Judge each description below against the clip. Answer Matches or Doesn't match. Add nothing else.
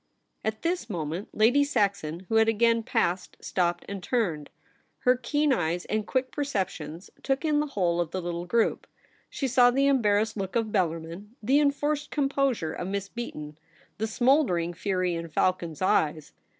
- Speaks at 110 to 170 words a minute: Matches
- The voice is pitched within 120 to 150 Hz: Doesn't match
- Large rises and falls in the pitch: Matches